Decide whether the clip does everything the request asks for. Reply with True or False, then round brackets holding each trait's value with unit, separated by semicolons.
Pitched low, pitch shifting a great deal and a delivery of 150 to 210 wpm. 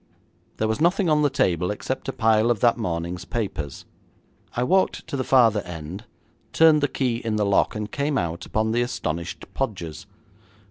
True (110 Hz; 6.5 semitones; 180 wpm)